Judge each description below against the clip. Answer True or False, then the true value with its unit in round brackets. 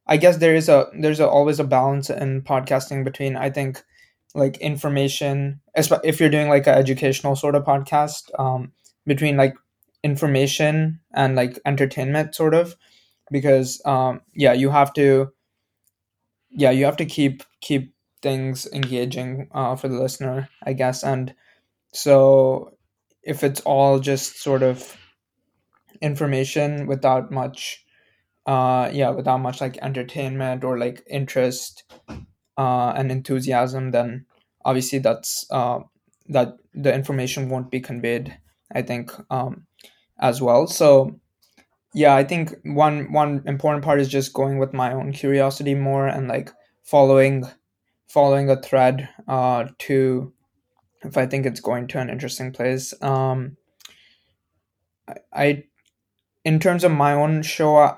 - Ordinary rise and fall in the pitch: False (1.8 semitones)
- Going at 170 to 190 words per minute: False (140 wpm)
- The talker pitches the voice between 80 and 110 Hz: False (135 Hz)